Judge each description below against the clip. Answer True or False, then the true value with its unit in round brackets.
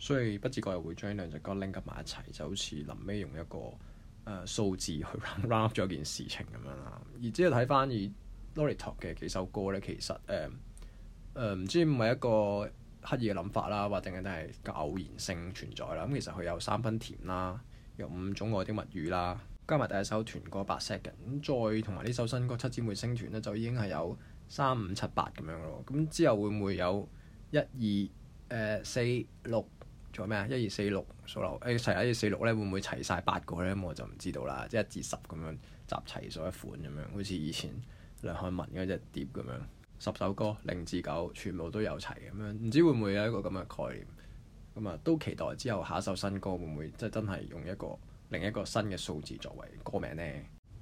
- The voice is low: True (105 Hz)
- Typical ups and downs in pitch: True (3.8 semitones)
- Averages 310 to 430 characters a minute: True (320 characters per minute)